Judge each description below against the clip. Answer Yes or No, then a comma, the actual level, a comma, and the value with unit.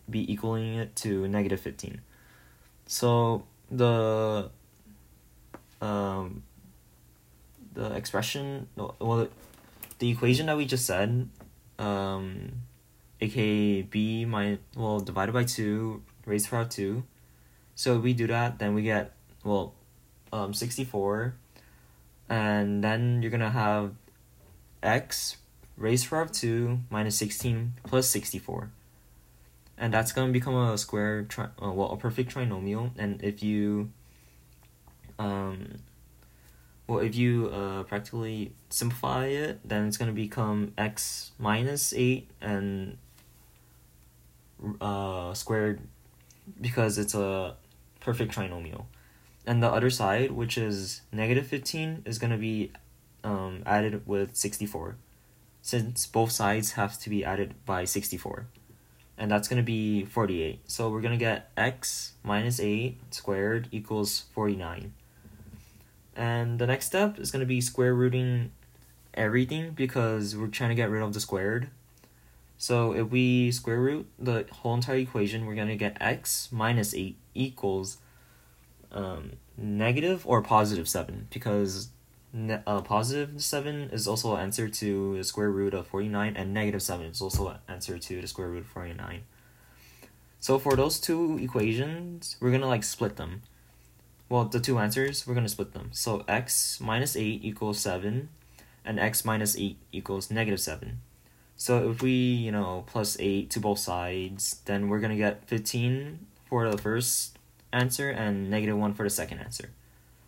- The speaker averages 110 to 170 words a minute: Yes, average, 145 wpm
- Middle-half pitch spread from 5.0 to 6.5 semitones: No, average, 3.3 semitones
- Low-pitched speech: Yes, low, 105 Hz